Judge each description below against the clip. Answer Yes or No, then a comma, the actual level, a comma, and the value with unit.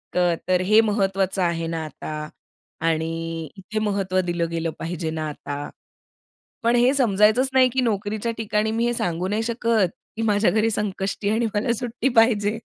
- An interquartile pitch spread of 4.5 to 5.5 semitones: Yes, average, 4.8 semitones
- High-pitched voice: Yes, high, 205 Hz